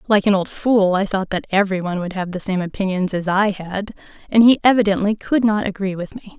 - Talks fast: Yes, fast, 235 wpm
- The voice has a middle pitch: No, high, 195 Hz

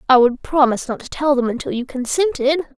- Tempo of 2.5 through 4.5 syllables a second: No, 6.1 syllables/s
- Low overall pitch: No, very high, 270 Hz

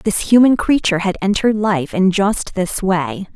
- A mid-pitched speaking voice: No, high, 195 Hz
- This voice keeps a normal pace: Yes, average, 180 wpm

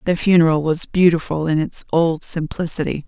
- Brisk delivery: No, average, 155 wpm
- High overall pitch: No, medium, 165 Hz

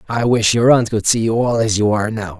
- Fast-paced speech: Yes, fast, 300 wpm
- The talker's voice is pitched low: Yes, low, 110 Hz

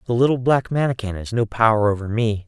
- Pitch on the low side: Yes, low, 115 Hz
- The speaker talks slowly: No, fast, 220 wpm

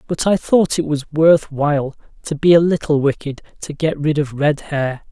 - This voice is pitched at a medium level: Yes, medium, 150 Hz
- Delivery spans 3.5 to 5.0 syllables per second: Yes, 4.7 syllables/s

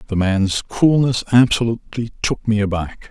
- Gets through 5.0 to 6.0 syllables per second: No, 4.8 syllables/s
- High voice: No, low, 110 Hz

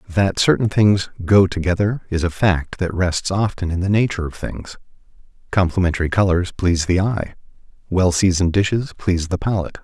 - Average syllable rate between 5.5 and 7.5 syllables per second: Yes, 5.6 syllables/s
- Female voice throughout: No, male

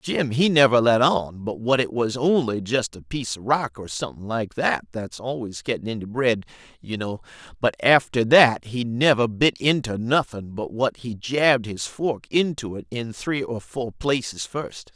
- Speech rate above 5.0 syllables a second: No, 4.5 syllables/s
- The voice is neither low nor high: No, low, 120 Hz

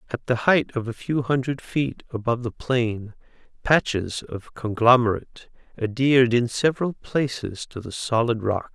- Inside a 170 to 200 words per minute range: No, average, 150 wpm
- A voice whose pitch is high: No, low, 125 Hz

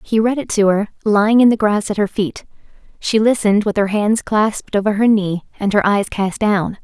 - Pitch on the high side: Yes, high, 210 Hz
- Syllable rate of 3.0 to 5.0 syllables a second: No, 5.3 syllables/s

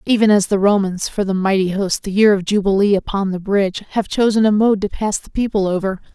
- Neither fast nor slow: No, fast, 235 wpm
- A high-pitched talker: Yes, high, 200 Hz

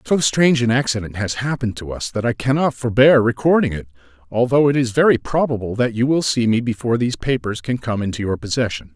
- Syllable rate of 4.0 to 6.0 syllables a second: No, 6.2 syllables/s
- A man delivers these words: Yes, male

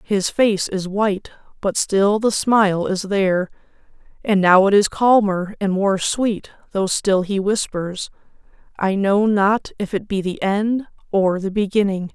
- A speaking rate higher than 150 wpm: Yes, average, 165 wpm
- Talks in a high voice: Yes, high, 200 Hz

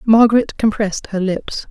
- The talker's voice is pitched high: Yes, high, 210 Hz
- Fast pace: No, average, 140 wpm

